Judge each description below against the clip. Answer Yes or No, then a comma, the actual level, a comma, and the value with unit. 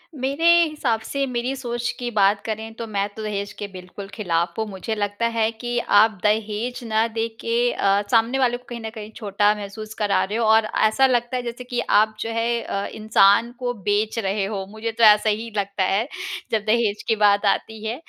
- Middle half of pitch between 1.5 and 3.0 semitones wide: Yes, narrow, 2.4 semitones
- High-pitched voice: Yes, high, 220 Hz